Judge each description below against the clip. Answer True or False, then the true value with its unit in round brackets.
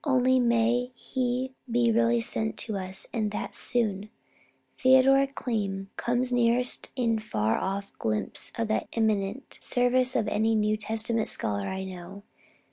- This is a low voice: False (225 Hz)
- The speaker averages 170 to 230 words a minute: False (140 wpm)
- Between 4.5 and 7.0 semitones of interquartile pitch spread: False (3.5 semitones)